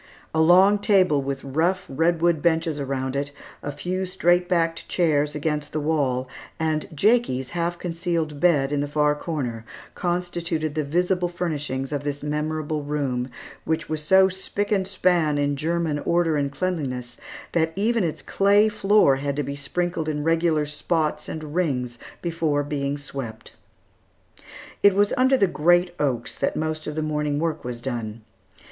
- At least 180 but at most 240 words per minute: No, average, 160 wpm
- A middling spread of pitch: Yes, average, 3.4 semitones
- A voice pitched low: No, medium, 155 Hz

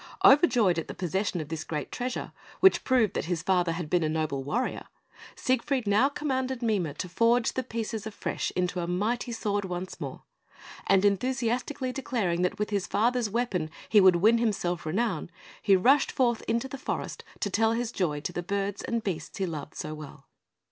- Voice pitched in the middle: No, high, 205 Hz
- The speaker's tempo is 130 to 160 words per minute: No, average, 190 wpm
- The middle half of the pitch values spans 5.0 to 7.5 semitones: Yes, average, 5.3 semitones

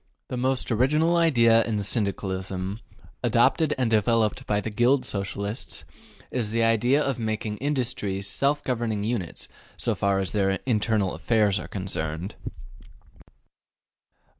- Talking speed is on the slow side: Yes, slow, 125 wpm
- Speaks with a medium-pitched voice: No, low, 110 Hz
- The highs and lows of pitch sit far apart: No, average, 3.8 semitones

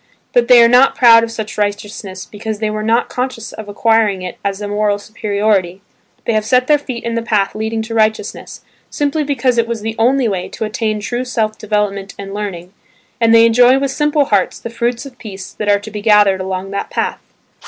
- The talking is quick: Yes, fast, 215 wpm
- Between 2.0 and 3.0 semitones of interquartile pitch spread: Yes, narrow, 2.5 semitones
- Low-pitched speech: No, high, 220 Hz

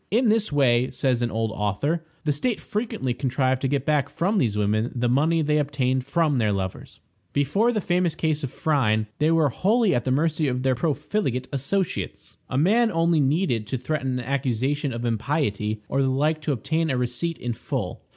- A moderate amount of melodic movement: Yes, average, 4.7 semitones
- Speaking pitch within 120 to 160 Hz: Yes, medium, 140 Hz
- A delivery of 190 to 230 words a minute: Yes, average, 195 wpm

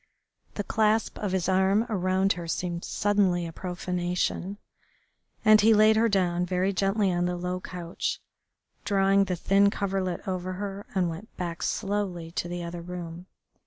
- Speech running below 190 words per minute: Yes, average, 160 wpm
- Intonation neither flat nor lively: No, narrow, 2.2 semitones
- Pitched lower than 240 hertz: Yes, medium, 185 Hz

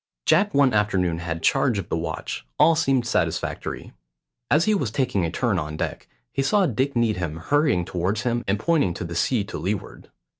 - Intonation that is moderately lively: No, wide, 7.7 semitones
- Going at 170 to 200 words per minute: Yes, average, 190 wpm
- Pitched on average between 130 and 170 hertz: No, low, 110 Hz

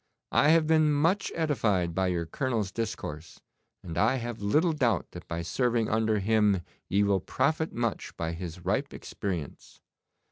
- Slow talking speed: No, average, 155 wpm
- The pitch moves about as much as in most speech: No, wide, 7.1 semitones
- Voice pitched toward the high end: No, low, 110 Hz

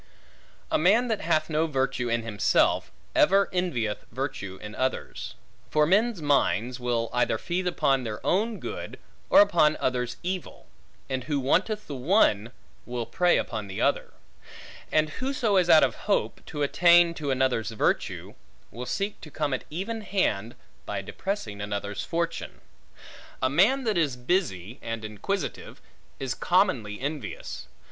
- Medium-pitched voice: Yes, medium, 145 Hz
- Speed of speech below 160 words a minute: Yes, average, 150 wpm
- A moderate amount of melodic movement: No, wide, 7.4 semitones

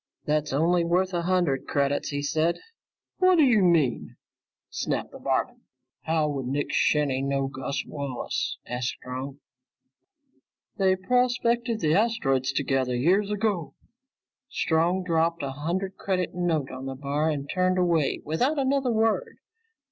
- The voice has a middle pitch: Yes, medium, 165 Hz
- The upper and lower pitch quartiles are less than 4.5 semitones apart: No, average, 5.3 semitones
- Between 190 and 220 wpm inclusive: No, slow, 135 wpm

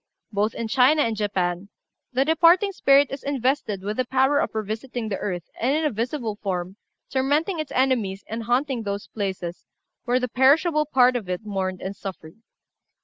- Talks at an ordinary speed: Yes, average, 175 wpm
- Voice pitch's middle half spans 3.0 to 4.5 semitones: No, wide, 5.4 semitones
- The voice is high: Yes, high, 240 Hz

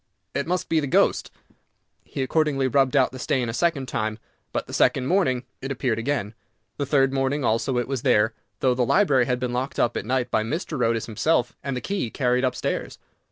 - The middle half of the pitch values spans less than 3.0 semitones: Yes, narrow, 2.4 semitones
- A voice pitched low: Yes, low, 130 Hz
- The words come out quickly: Yes, fast, 210 wpm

